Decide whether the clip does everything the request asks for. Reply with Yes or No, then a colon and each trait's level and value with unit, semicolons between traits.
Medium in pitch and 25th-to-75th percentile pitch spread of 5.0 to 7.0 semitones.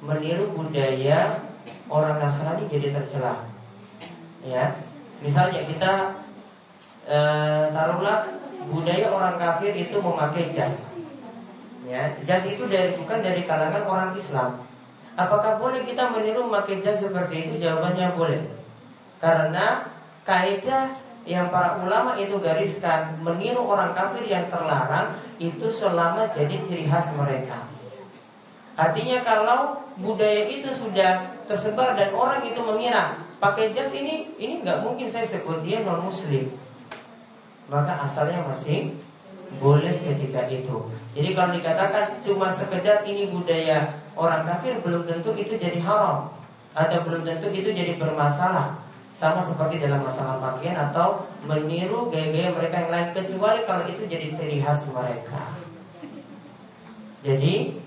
Yes: medium, 175 Hz; wide, 5.4 semitones